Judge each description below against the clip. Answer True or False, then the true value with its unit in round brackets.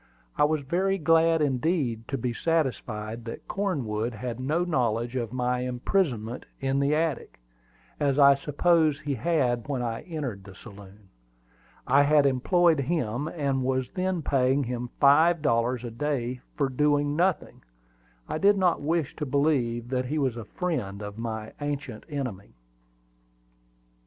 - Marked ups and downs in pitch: False (4.5 semitones)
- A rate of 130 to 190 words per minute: True (150 wpm)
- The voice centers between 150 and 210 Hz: False (135 Hz)